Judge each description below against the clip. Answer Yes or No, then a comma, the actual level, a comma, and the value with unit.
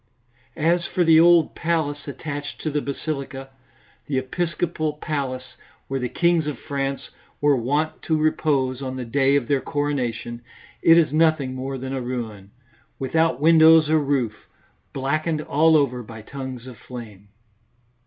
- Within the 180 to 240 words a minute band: No, average, 150 wpm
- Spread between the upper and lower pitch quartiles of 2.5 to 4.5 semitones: Yes, average, 3.3 semitones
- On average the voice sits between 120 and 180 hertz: Yes, medium, 140 Hz